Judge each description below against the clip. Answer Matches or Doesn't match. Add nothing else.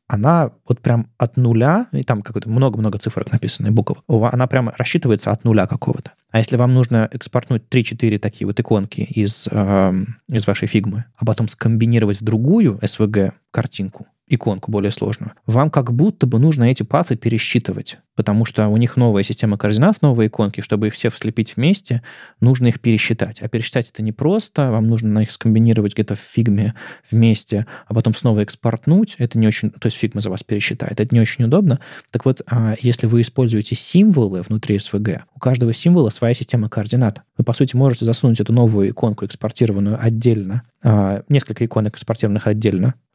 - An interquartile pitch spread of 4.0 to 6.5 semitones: Doesn't match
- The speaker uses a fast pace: Matches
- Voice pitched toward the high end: Doesn't match